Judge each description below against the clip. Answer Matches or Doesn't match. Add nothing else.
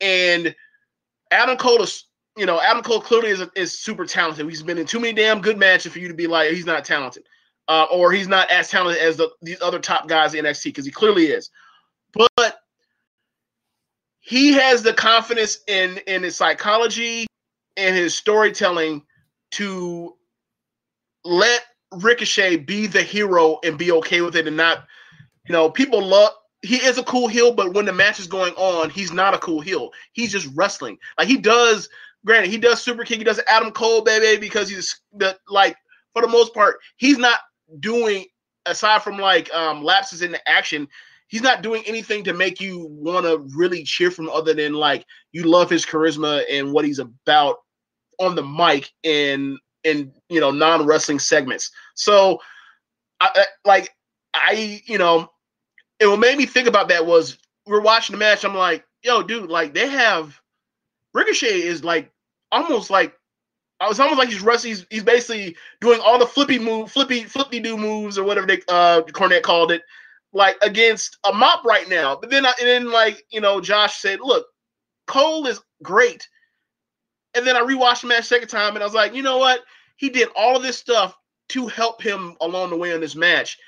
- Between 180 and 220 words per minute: Matches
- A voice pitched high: Matches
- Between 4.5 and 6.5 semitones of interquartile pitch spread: Matches